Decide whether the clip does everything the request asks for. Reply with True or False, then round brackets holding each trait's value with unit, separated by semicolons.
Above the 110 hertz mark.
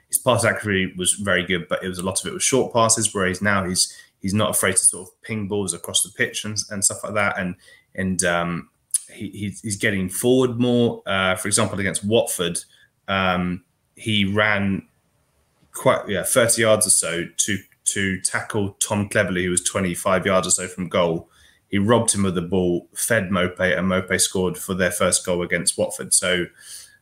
False (100 Hz)